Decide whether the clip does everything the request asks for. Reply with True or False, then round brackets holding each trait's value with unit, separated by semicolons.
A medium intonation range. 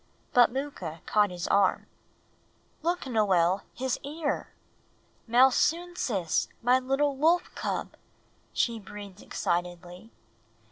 False (6.8 semitones)